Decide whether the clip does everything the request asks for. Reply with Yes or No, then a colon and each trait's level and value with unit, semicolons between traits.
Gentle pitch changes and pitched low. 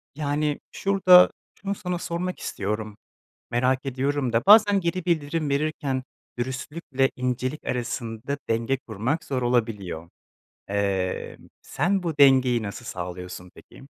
No: wide, 5.6 semitones; low, 130 Hz